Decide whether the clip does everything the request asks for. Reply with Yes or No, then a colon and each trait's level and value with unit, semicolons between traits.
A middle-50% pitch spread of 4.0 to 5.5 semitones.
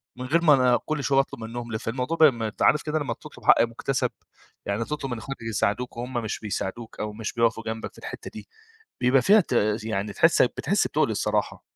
No: average, 3.4 semitones